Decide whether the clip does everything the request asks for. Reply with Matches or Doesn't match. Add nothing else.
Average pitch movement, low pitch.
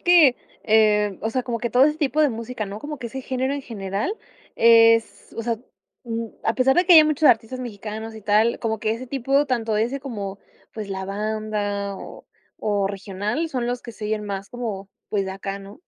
Doesn't match